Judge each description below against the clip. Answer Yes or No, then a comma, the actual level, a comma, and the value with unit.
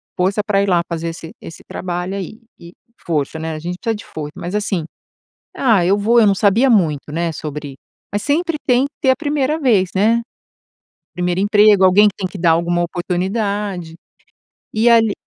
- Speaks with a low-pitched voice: No, high, 195 Hz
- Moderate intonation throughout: Yes, average, 4.2 semitones